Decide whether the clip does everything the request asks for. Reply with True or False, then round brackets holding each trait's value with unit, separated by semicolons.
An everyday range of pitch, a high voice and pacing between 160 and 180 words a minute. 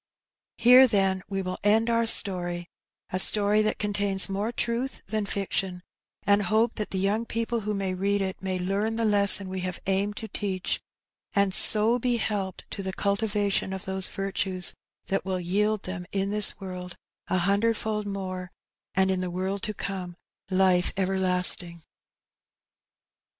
False (2.2 semitones; 195 Hz; 165 wpm)